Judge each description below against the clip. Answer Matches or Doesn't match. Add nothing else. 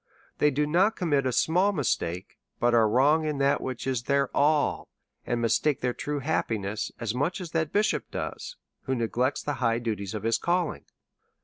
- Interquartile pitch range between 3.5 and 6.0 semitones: Matches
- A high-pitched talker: Doesn't match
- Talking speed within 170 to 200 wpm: Matches